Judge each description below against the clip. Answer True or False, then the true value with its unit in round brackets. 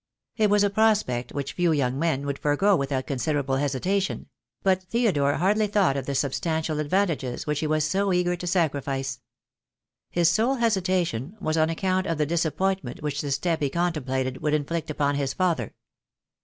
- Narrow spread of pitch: False (5.0 semitones)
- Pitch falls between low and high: True (160 Hz)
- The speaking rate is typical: True (185 wpm)